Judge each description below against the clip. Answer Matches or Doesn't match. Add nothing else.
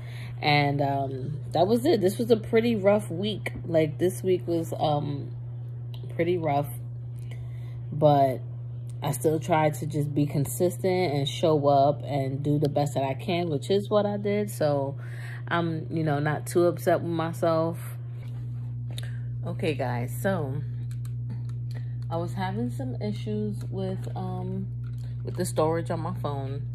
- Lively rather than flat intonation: Doesn't match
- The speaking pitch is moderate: Doesn't match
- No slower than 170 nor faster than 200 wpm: Doesn't match